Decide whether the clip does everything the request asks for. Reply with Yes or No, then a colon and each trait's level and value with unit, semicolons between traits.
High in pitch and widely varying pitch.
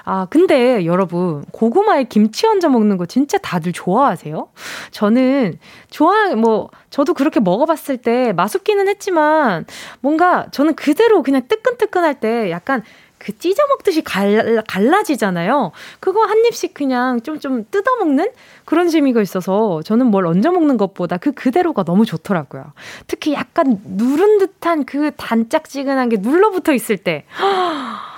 Yes: very high, 270 Hz; wide, 8.0 semitones